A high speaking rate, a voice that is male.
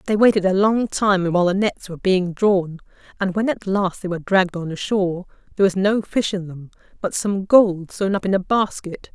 No: fast, 225 wpm; female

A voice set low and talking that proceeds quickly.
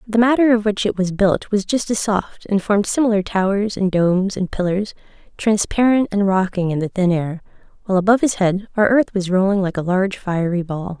No: high, 195 Hz; fast, 215 wpm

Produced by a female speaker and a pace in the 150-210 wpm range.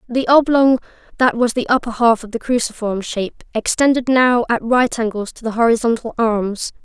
Yes: female; average, 175 wpm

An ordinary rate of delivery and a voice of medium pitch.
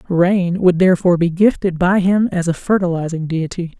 Yes: average, 175 wpm; medium, 180 Hz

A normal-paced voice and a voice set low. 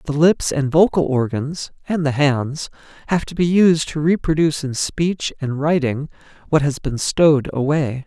No: average, 170 wpm; medium, 150 Hz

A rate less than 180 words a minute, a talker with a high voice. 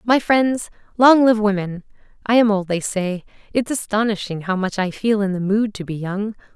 No: average, 200 wpm; high, 210 Hz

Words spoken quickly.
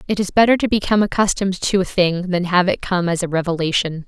Yes: fast, 235 wpm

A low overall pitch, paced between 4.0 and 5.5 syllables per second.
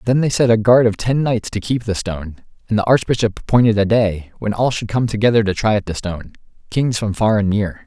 No: low, 110 Hz; 5.9 syllables/s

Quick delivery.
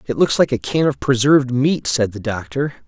Yes: fast, 230 wpm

